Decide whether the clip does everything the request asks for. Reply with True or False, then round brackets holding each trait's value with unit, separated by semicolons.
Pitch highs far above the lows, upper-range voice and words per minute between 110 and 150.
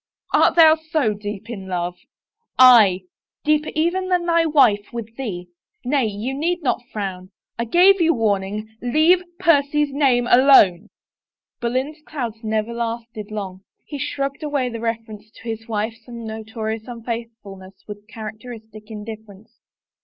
False (4.8 semitones; 230 Hz; 145 wpm)